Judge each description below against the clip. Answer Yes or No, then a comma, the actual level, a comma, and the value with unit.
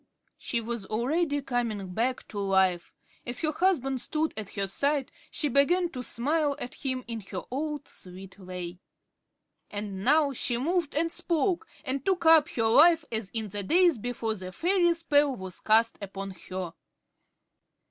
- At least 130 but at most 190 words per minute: Yes, average, 160 wpm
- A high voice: Yes, high, 245 Hz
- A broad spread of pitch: Yes, wide, 7.4 semitones